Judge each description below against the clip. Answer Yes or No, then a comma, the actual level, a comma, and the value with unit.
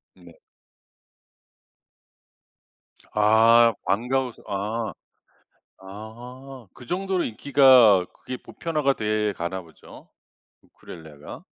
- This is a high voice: No, low, 110 Hz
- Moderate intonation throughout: Yes, average, 4.7 semitones